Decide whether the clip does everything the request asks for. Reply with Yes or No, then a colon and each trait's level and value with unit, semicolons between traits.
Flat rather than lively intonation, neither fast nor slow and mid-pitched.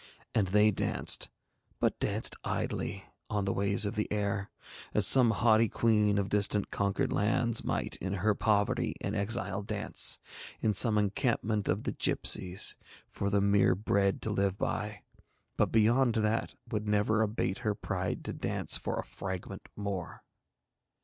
No: narrow, 1.6 semitones; average, 155 wpm; low, 105 Hz